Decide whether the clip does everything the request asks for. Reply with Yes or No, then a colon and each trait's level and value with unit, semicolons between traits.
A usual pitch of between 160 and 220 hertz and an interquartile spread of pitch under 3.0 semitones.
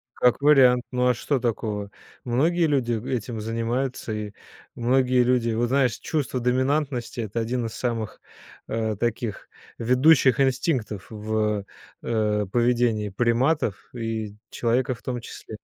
No: low, 120 Hz; narrow, 2.5 semitones